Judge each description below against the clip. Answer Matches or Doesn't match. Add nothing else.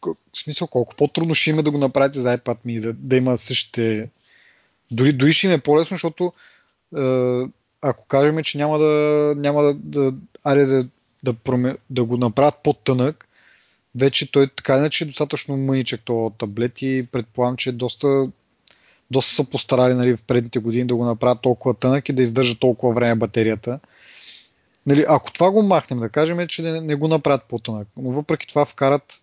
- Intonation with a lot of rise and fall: Doesn't match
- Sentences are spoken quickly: Matches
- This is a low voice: Matches